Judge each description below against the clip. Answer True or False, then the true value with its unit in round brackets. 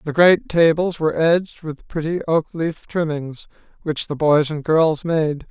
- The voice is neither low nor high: True (160 Hz)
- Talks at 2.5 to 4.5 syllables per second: True (4.4 syllables/s)